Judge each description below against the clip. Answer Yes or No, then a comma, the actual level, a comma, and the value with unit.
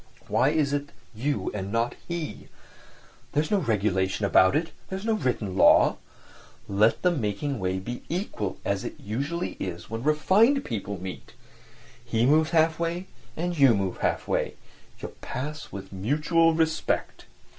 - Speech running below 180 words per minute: Yes, average, 150 wpm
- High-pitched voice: No, medium, 140 Hz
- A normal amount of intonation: No, wide, 8.1 semitones